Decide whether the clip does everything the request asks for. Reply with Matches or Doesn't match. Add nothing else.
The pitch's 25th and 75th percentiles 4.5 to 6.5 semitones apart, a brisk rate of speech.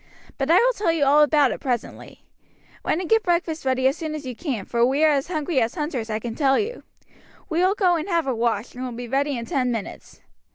Matches